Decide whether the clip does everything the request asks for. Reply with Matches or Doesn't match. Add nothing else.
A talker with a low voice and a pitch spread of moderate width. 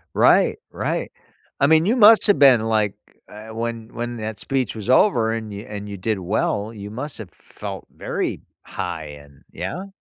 Matches